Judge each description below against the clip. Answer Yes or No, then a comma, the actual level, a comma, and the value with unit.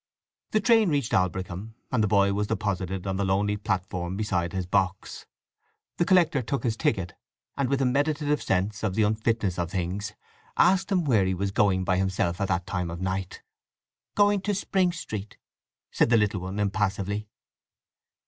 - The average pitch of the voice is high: No, low, 100 Hz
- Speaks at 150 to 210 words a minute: Yes, average, 175 wpm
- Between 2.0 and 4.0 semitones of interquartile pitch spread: No, average, 5.0 semitones